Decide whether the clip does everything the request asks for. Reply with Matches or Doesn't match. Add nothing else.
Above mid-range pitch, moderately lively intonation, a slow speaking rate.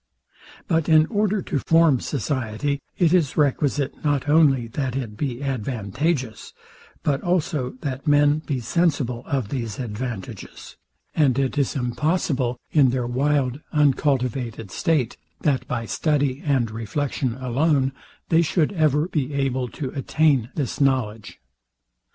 Doesn't match